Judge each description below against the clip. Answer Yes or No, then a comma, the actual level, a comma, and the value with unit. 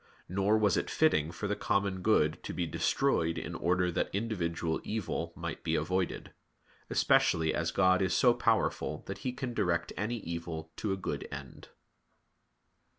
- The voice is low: Yes, very low, 90 Hz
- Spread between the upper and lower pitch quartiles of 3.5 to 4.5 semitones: Yes, average, 3.8 semitones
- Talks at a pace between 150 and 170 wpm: Yes, average, 160 wpm